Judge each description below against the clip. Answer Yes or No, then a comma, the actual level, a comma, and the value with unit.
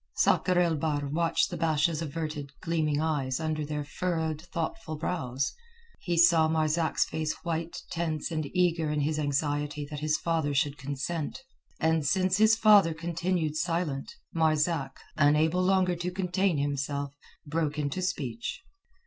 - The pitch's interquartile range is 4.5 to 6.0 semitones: No, narrow, 2.6 semitones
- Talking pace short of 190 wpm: Yes, average, 140 wpm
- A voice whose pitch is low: No, medium, 160 Hz